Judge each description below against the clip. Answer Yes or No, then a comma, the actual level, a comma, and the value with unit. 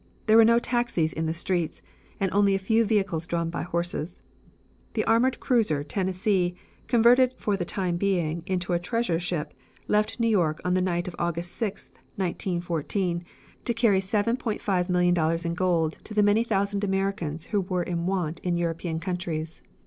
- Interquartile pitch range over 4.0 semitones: No, average, 3.3 semitones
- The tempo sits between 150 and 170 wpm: Yes, average, 165 wpm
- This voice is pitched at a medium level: Yes, medium, 180 Hz